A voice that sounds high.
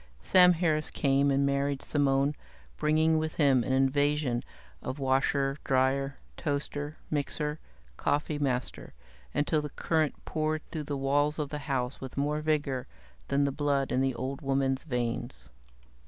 No: medium, 140 Hz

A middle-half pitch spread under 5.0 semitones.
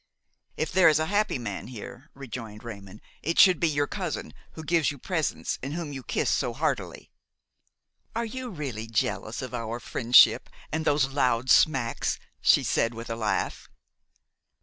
No: wide, 5.5 semitones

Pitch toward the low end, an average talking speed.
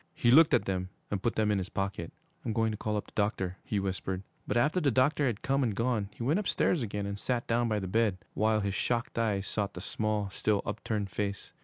No: low, 105 Hz; fast, 240 wpm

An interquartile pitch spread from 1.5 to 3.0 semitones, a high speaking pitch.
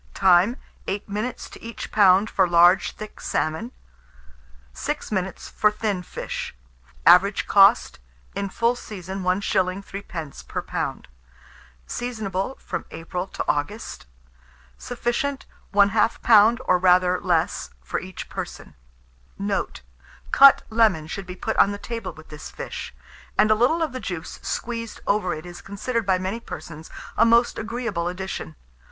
No: average, 3.9 semitones; high, 195 Hz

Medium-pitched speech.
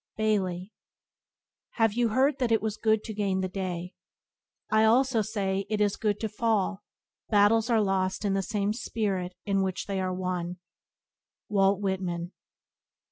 No: high, 205 Hz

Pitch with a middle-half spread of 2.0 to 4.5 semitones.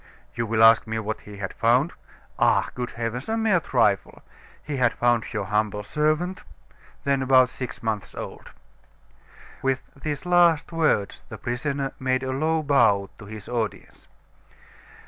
No: average, 4.9 semitones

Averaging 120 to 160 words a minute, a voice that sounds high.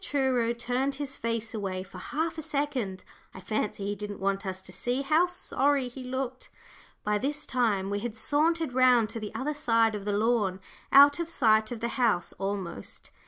No: average, 190 wpm; high, 235 Hz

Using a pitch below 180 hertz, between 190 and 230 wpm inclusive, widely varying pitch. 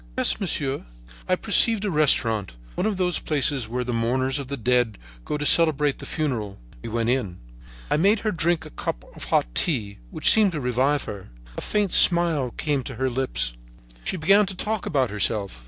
Yes: low, 135 Hz; average, 195 wpm; wide, 6.5 semitones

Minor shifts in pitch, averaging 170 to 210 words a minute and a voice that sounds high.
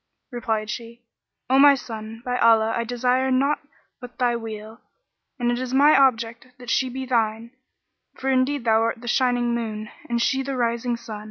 Yes: narrow, 2.2 semitones; average, 180 wpm; high, 240 Hz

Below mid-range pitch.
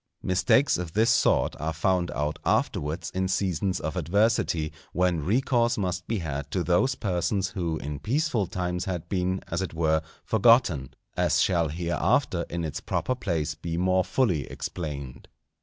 Yes: very low, 90 Hz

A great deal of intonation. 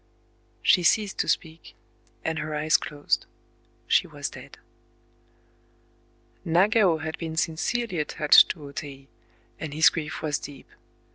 No: narrow, 2.4 semitones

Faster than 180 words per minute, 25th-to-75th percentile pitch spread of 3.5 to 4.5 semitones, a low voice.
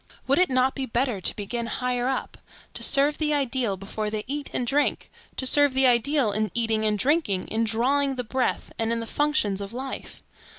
No: average, 200 wpm; average, 4.0 semitones; very high, 250 Hz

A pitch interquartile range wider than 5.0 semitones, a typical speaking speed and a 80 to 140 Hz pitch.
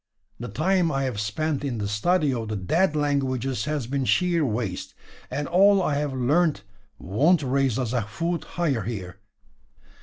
Yes: wide, 5.5 semitones; average, 170 wpm; low, 135 Hz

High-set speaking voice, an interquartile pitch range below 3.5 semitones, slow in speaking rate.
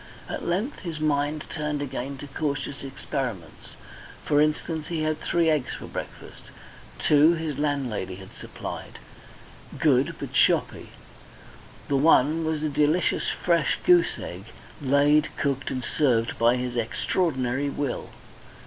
No: medium, 145 Hz; average, 3.0 semitones; slow, 130 wpm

